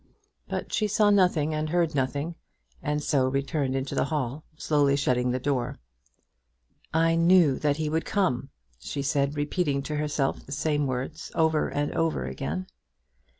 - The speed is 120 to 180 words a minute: Yes, average, 155 wpm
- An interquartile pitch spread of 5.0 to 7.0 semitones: No, average, 2.9 semitones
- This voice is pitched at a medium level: Yes, medium, 145 Hz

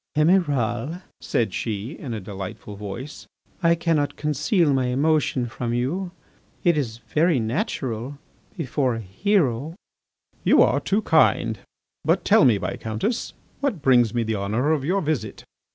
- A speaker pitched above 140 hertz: No, low, 135 Hz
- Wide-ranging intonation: Yes, wide, 5.9 semitones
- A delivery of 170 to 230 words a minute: No, average, 140 wpm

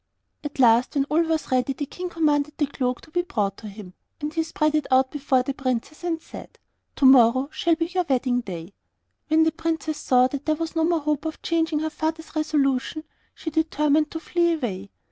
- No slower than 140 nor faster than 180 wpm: No, fast, 205 wpm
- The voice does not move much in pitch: No, average, 3.7 semitones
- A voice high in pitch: Yes, very high, 300 Hz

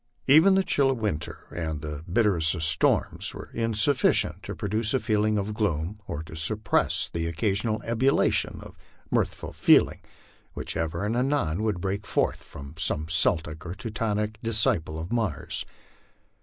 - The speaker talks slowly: No, average, 155 wpm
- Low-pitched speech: Yes, low, 105 Hz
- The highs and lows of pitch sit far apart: Yes, wide, 5.7 semitones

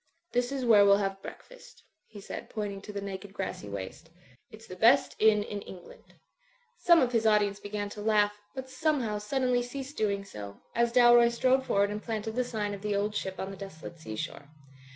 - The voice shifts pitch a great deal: No, average, 3.3 semitones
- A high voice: Yes, high, 210 Hz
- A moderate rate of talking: No, fast, 210 wpm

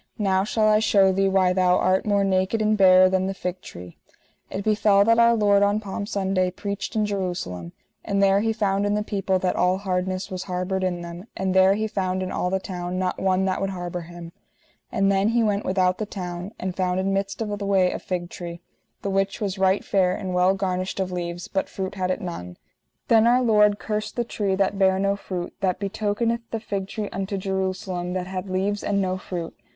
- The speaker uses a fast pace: Yes, fast, 220 wpm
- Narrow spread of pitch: Yes, narrow, 1.7 semitones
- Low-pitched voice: No, high, 190 Hz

